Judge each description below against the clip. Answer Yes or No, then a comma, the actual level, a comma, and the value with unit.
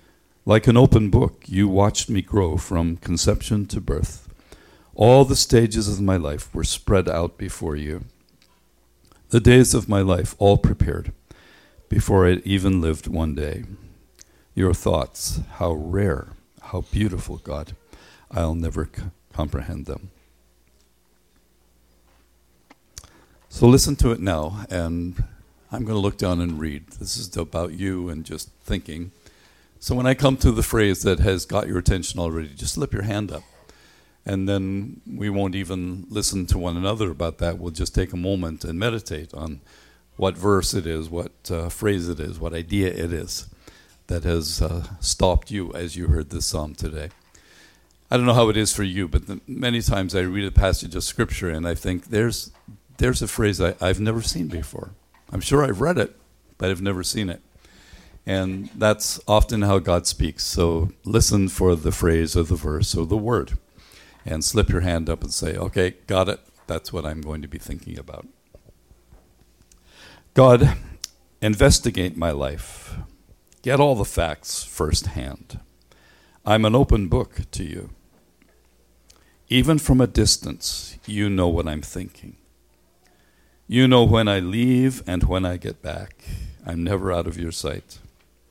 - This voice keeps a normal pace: Yes, average, 165 wpm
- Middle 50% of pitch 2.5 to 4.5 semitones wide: Yes, average, 4.0 semitones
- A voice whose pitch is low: Yes, very low, 90 Hz